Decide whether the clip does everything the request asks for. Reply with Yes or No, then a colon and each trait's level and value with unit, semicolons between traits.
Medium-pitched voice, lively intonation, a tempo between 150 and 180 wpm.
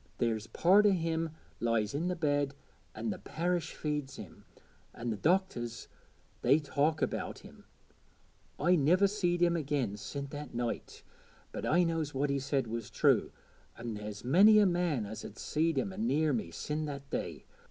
Yes: medium, 145 Hz; wide, 6.3 semitones; average, 170 wpm